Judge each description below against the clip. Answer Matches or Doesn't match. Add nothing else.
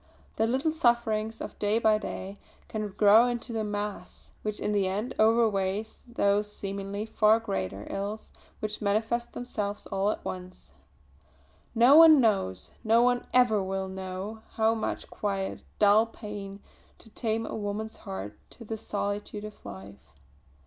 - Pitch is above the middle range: Matches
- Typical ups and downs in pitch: Doesn't match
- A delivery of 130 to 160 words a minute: Matches